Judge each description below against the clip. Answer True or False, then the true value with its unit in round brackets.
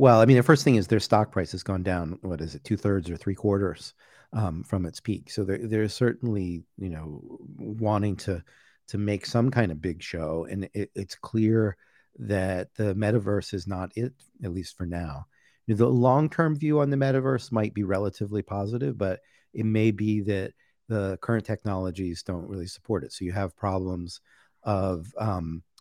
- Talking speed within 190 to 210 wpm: True (200 wpm)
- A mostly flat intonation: False (3.2 semitones)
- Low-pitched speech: True (100 Hz)